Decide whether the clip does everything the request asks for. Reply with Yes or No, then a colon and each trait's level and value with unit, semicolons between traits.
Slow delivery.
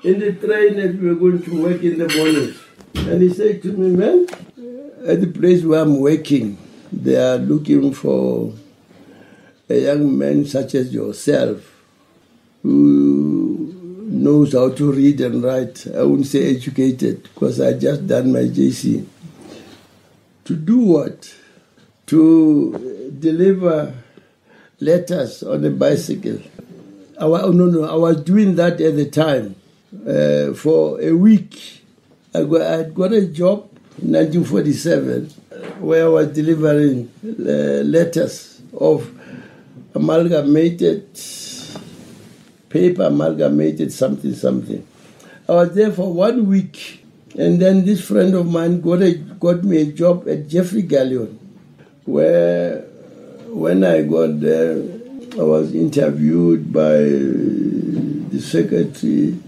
Yes: slow, 125 wpm